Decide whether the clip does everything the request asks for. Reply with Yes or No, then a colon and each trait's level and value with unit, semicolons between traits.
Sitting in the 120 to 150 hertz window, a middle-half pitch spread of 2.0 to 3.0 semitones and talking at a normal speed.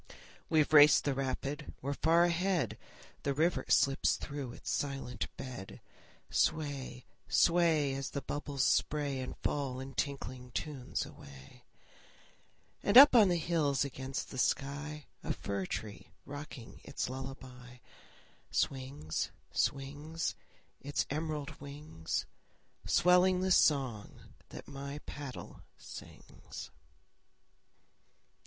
No: medium, 140 Hz; average, 2.7 semitones; slow, 110 wpm